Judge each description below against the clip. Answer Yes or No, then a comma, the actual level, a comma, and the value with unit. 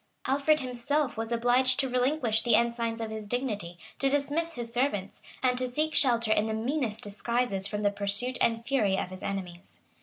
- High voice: Yes, high, 235 Hz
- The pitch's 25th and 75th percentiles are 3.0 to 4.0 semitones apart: Yes, average, 3.6 semitones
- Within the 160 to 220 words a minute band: Yes, average, 185 wpm